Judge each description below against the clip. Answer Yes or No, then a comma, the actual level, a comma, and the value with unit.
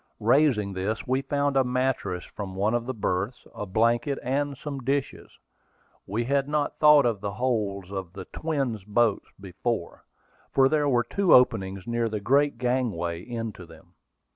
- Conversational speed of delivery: Yes, average, 165 wpm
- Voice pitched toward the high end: No, low, 120 Hz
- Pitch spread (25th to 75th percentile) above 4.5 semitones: Yes, average, 5.3 semitones